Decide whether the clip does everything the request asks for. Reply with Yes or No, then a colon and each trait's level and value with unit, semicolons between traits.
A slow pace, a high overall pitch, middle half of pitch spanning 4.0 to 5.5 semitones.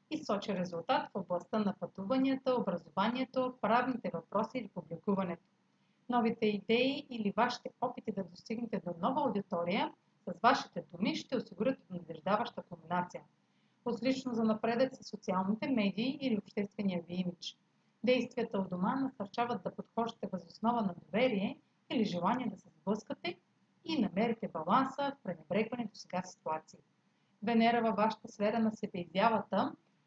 No: average, 135 wpm; high, 215 Hz; average, 4.4 semitones